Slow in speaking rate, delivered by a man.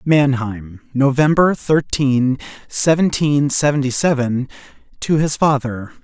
Yes: slow, 90 wpm; male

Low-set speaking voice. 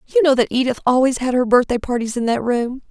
No: very high, 250 Hz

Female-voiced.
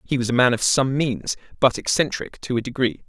No: male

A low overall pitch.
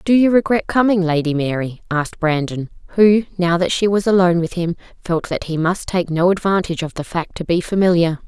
No: medium, 175 Hz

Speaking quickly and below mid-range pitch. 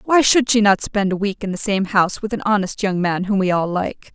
No: fast, 290 wpm; high, 200 Hz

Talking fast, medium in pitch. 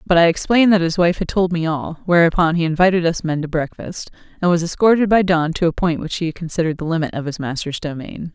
Yes: fast, 245 wpm; medium, 170 Hz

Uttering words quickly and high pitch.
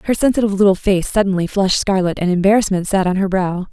Yes: fast, 210 wpm; high, 195 Hz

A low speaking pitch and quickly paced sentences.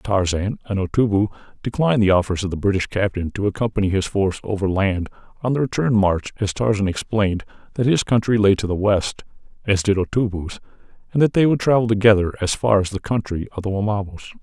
No: low, 105 Hz; average, 190 wpm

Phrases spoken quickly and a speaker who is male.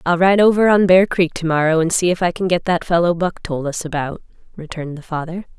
No: fast, 245 wpm; female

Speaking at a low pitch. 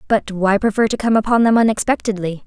No: high, 210 Hz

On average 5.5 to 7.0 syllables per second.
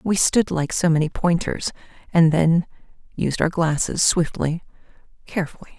No: 4.7 syllables/s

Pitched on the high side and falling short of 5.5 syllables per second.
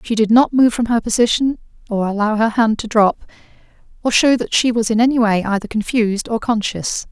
No: high, 225 Hz; 5.6 syllables/s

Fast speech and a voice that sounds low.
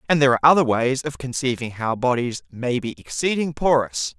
No: average, 185 wpm; low, 130 Hz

